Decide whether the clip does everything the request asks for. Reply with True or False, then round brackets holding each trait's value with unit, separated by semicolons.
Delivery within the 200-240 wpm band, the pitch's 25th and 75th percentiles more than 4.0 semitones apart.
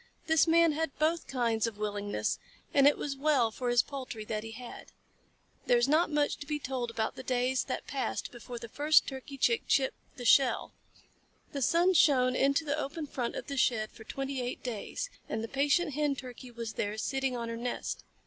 False (205 wpm; 3.6 semitones)